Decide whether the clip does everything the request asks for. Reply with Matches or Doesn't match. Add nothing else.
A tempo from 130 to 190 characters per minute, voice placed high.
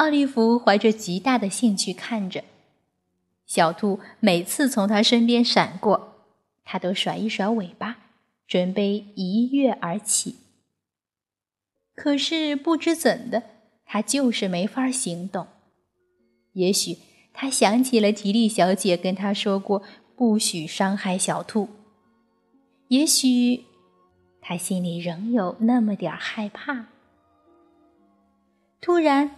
Matches